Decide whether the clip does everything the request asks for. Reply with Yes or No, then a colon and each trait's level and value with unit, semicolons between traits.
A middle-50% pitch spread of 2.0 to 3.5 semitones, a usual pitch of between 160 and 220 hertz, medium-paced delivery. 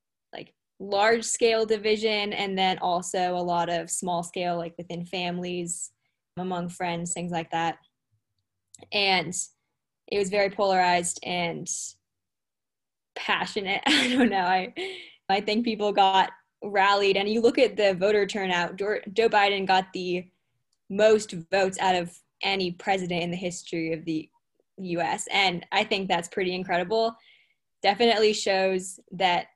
No: average, 2.7 semitones; medium, 185 Hz; slow, 130 wpm